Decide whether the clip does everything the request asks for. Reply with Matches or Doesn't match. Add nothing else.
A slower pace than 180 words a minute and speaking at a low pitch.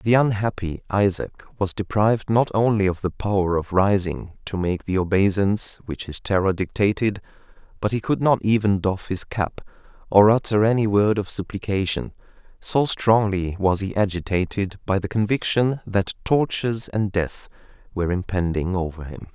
Matches